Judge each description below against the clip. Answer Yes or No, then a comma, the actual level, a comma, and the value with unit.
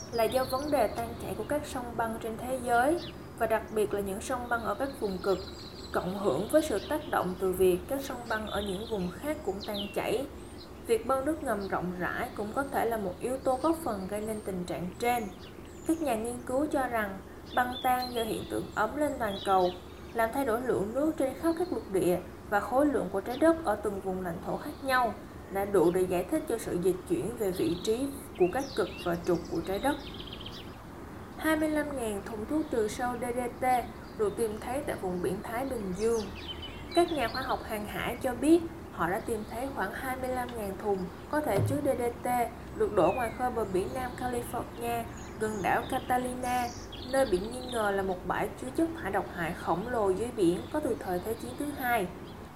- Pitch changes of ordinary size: No, wide, 5.7 semitones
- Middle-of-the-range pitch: No, high, 240 Hz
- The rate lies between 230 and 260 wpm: No, average, 215 wpm